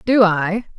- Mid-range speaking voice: No, high, 200 Hz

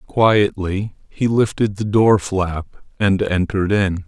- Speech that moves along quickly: No, slow, 135 wpm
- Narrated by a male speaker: Yes, male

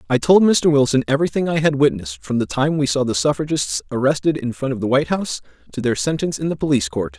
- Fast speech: Yes, fast, 240 wpm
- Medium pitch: Yes, medium, 145 Hz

